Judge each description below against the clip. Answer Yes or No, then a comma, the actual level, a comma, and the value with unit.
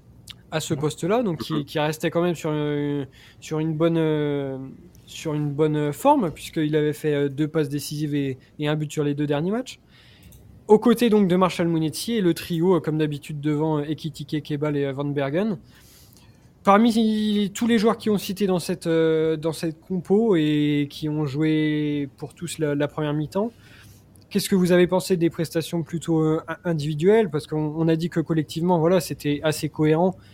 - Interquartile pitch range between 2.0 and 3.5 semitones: Yes, average, 3.1 semitones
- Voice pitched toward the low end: No, medium, 155 Hz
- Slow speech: No, average, 180 wpm